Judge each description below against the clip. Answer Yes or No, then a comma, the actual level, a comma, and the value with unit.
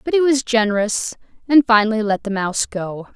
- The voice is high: Yes, high, 225 Hz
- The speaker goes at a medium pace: Yes, average, 190 wpm